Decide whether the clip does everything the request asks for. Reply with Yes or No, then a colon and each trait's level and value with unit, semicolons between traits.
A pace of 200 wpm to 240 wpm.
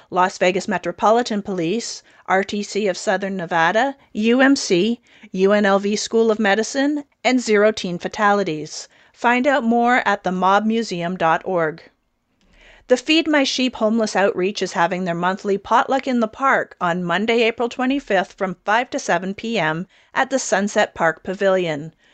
No: average, 140 wpm